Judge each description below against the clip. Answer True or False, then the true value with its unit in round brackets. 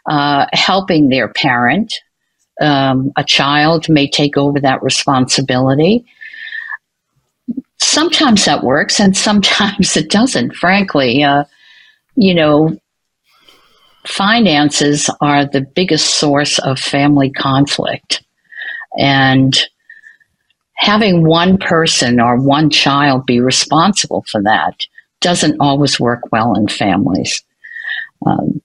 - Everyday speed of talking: False (105 wpm)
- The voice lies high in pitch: False (155 Hz)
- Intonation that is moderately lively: False (7.1 semitones)